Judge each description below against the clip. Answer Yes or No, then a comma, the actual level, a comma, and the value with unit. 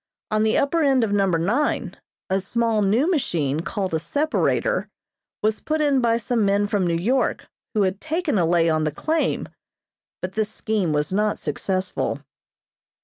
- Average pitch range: No, wide, 5.8 semitones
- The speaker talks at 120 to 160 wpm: No, average, 170 wpm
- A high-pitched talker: Yes, high, 210 Hz